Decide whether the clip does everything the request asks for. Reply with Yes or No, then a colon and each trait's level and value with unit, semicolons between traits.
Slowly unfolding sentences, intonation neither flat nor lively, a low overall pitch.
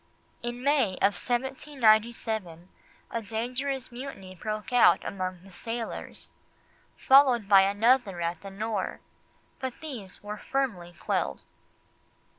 No: slow, 110 wpm; average, 4.6 semitones; high, 220 Hz